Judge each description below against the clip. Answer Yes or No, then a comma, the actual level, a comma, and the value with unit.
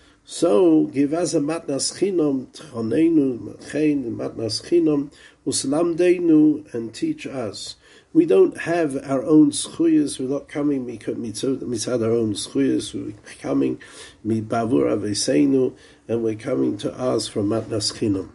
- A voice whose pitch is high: No, medium, 145 Hz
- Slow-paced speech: Yes, slow, 125 wpm